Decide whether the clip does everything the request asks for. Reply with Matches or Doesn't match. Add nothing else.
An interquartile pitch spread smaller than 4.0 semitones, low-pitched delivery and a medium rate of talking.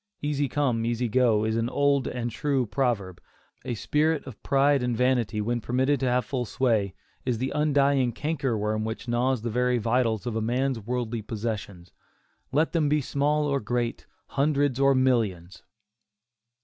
Matches